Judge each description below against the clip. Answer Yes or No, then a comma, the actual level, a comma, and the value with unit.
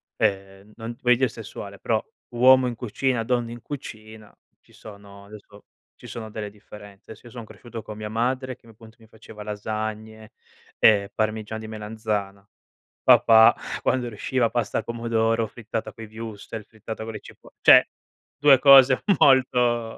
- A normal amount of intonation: No, narrow, 2.0 semitones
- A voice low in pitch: Yes, low, 110 Hz